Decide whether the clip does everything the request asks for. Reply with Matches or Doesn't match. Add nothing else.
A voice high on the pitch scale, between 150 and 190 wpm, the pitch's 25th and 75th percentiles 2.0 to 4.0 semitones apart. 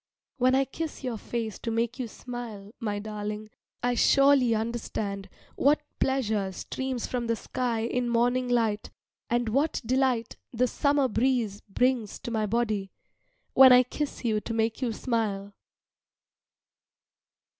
Doesn't match